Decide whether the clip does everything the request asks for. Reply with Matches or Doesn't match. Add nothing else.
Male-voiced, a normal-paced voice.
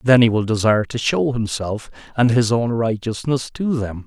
Matches